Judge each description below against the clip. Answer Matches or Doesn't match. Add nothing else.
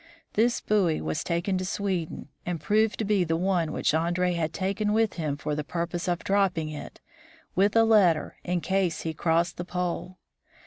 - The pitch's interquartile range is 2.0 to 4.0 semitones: Matches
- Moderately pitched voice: Matches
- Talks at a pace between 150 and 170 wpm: Doesn't match